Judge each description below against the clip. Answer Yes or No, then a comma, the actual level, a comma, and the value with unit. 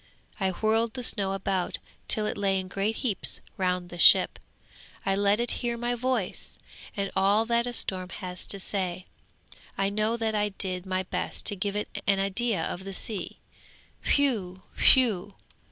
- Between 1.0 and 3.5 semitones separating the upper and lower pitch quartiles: Yes, average, 3.0 semitones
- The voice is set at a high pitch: Yes, high, 200 Hz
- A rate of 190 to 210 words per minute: No, average, 170 wpm